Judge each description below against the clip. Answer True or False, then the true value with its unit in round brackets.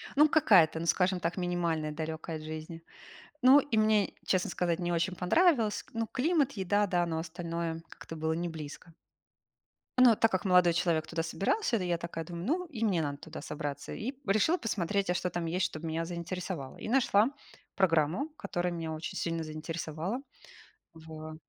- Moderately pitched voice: True (175 Hz)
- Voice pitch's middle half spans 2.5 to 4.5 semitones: True (4.1 semitones)